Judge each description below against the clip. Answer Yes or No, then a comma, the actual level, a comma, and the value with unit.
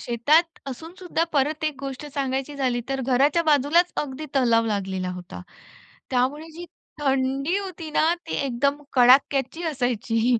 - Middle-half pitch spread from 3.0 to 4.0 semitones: Yes, average, 3.7 semitones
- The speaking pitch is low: No, very high, 275 Hz